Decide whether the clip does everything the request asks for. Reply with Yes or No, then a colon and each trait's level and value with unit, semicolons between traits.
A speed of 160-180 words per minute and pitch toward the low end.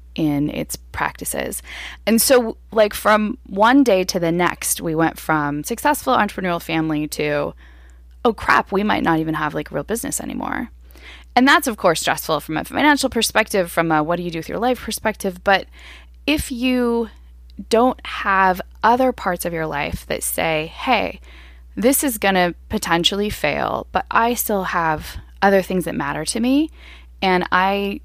No: average, 170 wpm; medium, 180 Hz